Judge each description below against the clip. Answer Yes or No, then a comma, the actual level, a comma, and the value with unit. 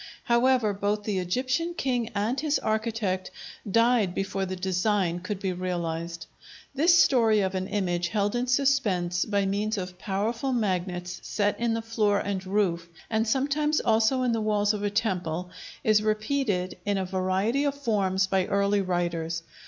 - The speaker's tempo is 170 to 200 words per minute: No, average, 160 wpm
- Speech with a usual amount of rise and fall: Yes, average, 3.7 semitones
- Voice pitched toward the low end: No, high, 205 Hz